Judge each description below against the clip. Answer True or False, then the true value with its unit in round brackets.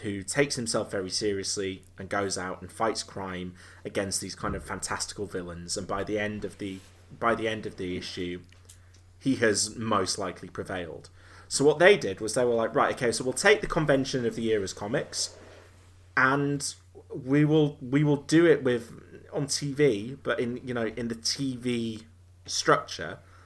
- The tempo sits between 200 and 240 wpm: False (185 wpm)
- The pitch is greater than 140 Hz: False (105 Hz)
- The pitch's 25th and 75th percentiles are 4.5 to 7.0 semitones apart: True (5.1 semitones)